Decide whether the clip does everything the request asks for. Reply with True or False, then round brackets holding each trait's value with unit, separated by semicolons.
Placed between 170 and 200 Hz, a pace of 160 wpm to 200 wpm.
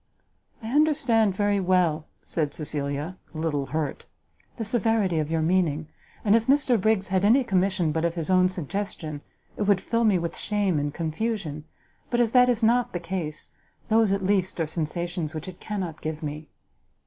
True (185 Hz; 180 wpm)